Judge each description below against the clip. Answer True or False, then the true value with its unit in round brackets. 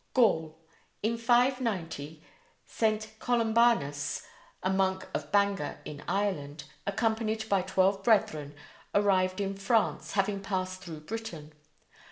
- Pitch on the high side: True (195 Hz)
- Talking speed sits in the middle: False (110 wpm)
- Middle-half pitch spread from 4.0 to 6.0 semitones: True (4.8 semitones)